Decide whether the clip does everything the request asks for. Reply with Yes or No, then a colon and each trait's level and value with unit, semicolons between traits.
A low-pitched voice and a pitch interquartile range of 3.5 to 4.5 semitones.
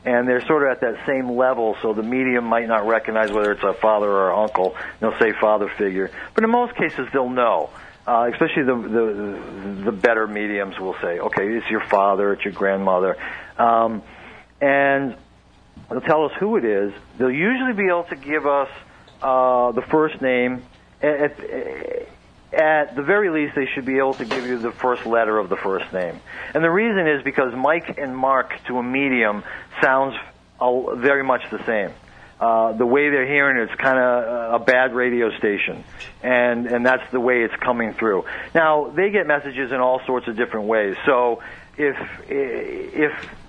Yes: low, 125 Hz; average, 3.9 semitones